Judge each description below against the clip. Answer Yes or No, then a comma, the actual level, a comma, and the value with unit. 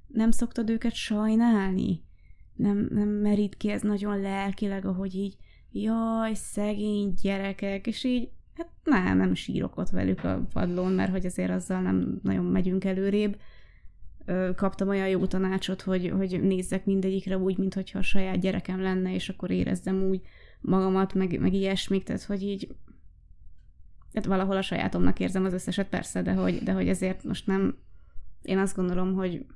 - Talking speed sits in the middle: No, fast, 160 wpm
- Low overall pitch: No, high, 190 Hz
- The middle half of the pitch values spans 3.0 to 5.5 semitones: No, narrow, 2.4 semitones